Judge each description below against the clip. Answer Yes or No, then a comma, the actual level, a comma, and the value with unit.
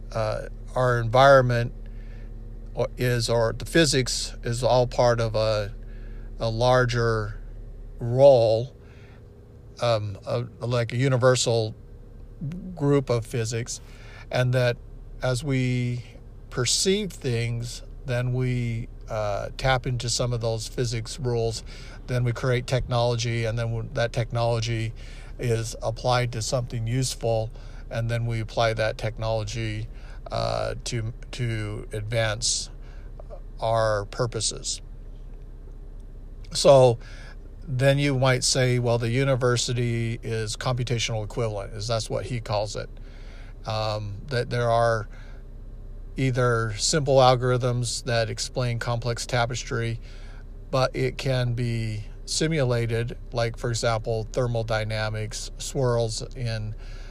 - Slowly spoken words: Yes, slow, 110 wpm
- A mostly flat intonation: Yes, narrow, 2.0 semitones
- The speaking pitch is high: No, low, 115 Hz